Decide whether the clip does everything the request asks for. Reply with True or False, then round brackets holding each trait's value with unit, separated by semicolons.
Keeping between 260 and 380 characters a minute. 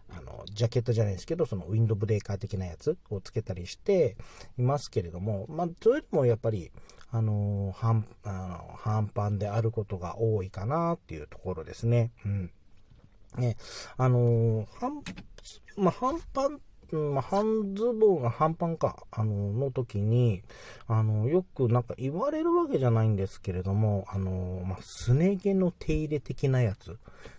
True (335 characters per minute)